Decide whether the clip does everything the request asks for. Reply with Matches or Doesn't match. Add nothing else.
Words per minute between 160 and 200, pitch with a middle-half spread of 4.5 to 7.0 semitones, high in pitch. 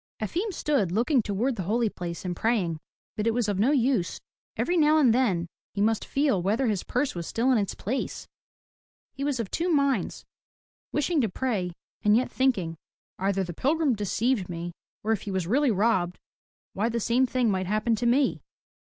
Matches